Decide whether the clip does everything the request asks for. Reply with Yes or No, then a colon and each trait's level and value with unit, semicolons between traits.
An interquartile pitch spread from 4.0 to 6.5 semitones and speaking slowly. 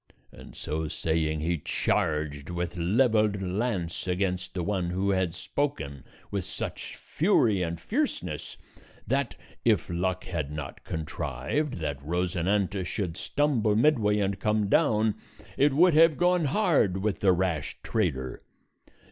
Yes: average, 4.7 semitones; slow, 130 wpm